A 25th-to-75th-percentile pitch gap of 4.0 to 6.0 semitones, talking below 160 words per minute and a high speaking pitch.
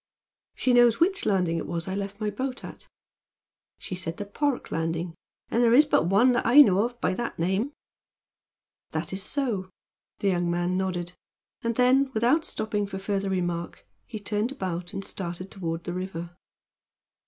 No: average, 5.3 semitones; average, 175 wpm; high, 195 Hz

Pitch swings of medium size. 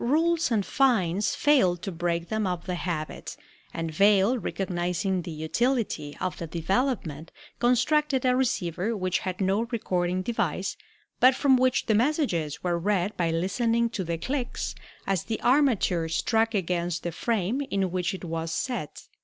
No: wide, 5.7 semitones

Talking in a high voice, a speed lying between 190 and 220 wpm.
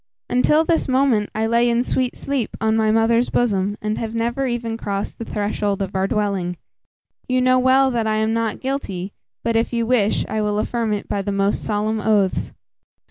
Yes: high, 225 Hz; average, 195 wpm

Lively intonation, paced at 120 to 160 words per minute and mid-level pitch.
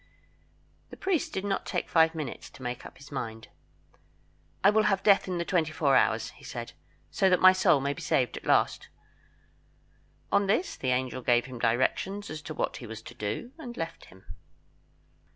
No: wide, 7.4 semitones; average, 190 wpm; medium, 155 Hz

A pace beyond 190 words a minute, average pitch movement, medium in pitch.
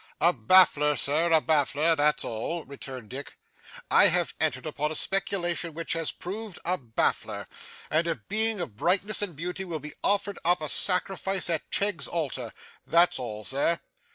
No: average, 165 wpm; average, 3.9 semitones; medium, 165 Hz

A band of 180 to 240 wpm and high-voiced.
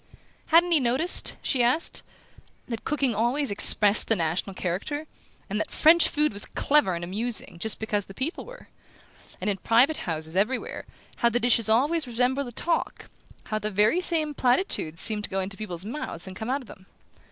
Yes: average, 185 wpm; high, 235 Hz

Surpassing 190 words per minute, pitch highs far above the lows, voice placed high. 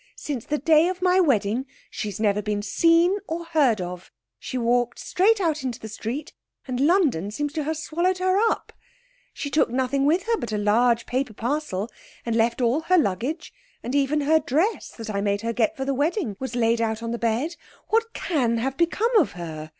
Yes: fast, 205 wpm; wide, 6.1 semitones; very high, 265 Hz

